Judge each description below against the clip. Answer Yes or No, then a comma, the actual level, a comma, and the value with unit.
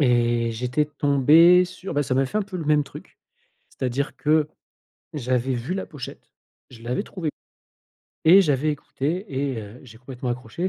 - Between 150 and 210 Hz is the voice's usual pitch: No, medium, 140 Hz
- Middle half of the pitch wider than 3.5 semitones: Yes, average, 4.1 semitones